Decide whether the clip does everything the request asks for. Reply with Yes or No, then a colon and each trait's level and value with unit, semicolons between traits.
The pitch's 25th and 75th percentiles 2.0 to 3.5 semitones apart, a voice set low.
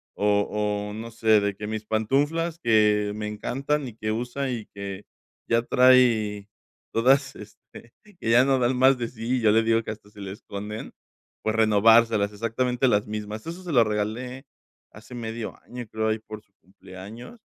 Yes: average, 2.9 semitones; low, 110 Hz